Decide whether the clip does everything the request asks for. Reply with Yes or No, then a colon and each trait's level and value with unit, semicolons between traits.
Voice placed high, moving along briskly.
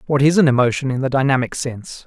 No: low, 135 Hz; fast, 235 wpm